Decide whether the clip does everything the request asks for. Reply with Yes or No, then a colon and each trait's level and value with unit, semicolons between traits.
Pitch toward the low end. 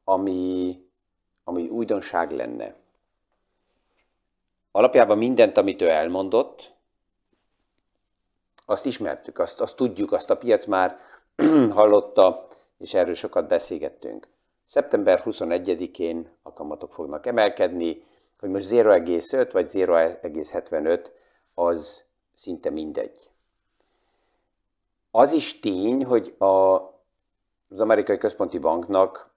Yes: low, 100 Hz